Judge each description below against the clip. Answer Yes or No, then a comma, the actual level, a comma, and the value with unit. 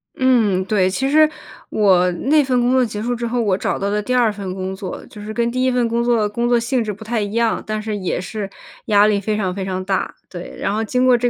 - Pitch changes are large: No, average, 3.3 semitones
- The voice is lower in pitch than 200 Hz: No, high, 215 Hz